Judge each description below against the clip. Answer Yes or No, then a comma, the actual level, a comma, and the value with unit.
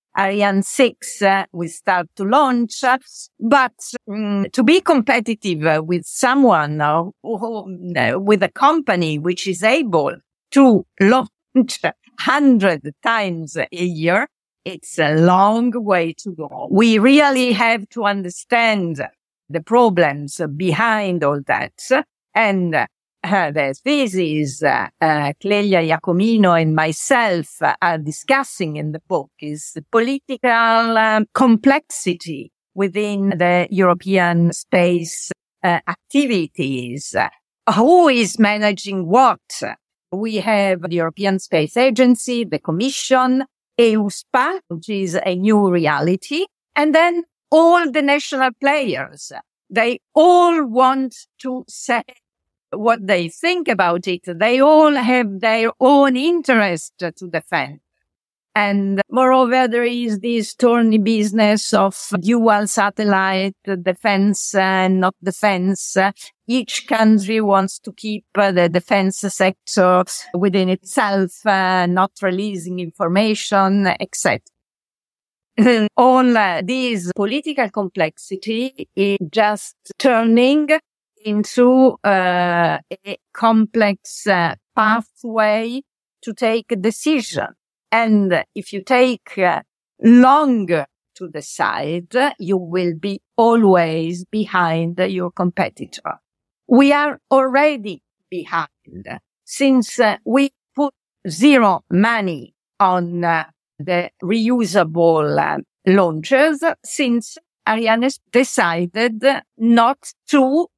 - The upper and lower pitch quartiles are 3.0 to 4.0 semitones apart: No, wide, 5.5 semitones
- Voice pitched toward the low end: No, high, 205 Hz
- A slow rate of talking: Yes, slow, 110 wpm